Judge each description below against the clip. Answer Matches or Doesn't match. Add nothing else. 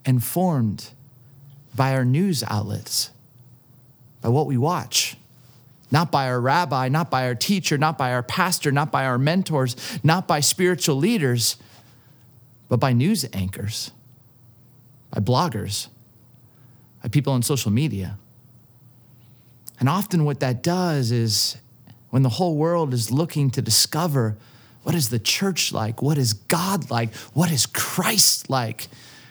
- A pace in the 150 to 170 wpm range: Doesn't match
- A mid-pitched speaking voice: Doesn't match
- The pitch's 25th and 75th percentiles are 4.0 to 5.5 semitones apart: Doesn't match